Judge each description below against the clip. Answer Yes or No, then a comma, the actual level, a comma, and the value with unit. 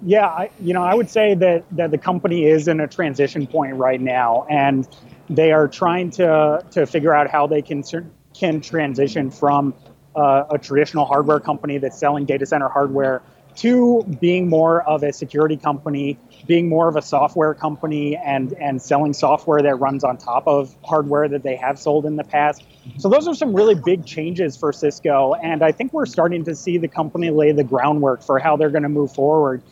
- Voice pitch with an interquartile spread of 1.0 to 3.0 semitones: Yes, average, 2.7 semitones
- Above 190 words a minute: Yes, average, 200 wpm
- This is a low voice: No, medium, 150 Hz